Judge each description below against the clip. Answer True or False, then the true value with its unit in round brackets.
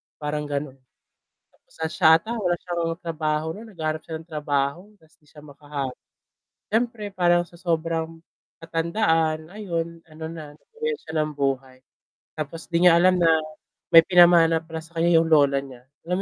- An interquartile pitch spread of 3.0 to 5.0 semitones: False (2.4 semitones)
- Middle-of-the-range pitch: True (165 Hz)